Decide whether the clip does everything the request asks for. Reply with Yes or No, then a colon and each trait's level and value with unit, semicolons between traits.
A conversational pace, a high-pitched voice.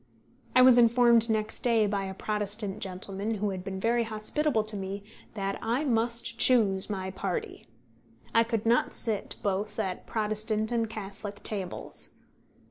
Yes: average, 150 wpm; high, 215 Hz